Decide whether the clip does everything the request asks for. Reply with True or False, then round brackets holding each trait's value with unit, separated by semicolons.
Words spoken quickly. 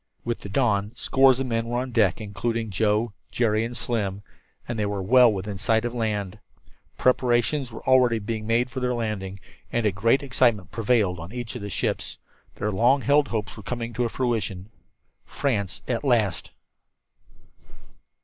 False (170 wpm)